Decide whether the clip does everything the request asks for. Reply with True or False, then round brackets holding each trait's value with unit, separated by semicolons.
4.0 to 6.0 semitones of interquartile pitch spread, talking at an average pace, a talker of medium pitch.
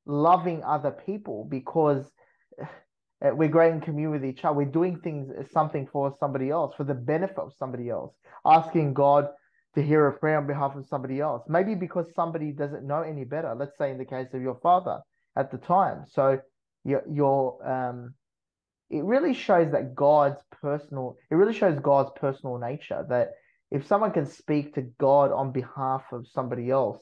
False (3.1 semitones; 180 wpm; 145 Hz)